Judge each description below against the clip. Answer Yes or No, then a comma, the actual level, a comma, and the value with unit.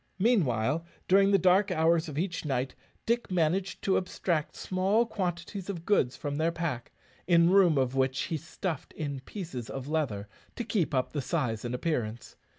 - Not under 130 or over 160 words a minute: No, average, 170 wpm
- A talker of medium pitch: Yes, medium, 165 Hz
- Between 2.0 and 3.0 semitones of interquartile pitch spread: No, wide, 5.6 semitones